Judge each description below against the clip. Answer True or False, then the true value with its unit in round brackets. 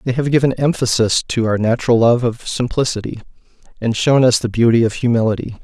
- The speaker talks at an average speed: True (180 wpm)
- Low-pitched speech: True (120 Hz)